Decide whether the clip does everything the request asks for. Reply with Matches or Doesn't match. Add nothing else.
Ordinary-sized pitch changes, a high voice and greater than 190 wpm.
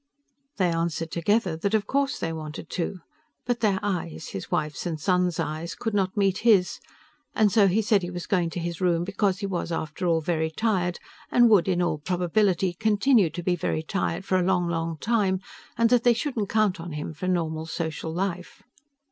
Doesn't match